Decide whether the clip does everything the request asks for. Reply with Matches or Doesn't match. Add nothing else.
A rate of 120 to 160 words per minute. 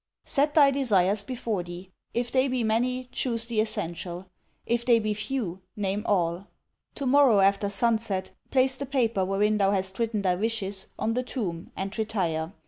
Doesn't match